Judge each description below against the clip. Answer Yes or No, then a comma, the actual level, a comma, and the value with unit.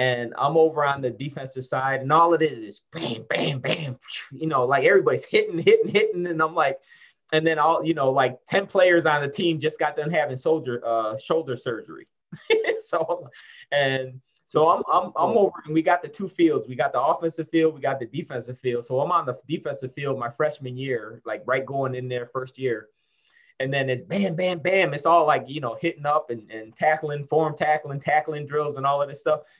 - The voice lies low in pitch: No, medium, 150 Hz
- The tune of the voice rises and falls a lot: No, average, 4.1 semitones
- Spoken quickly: Yes, fast, 215 wpm